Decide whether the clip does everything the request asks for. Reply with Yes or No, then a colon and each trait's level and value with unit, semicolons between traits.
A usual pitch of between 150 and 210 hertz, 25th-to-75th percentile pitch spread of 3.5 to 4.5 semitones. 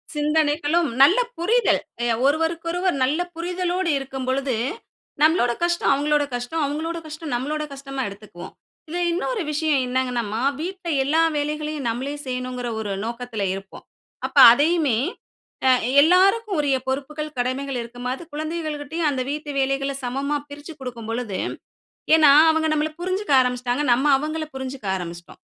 No: very high, 290 Hz; average, 4.0 semitones